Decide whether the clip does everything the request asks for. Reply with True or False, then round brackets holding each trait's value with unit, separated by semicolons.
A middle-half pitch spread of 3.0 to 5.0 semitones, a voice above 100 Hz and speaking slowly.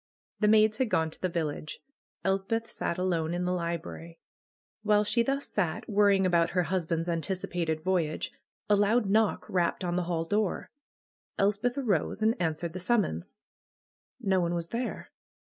False (3.8 semitones; 185 Hz; 160 wpm)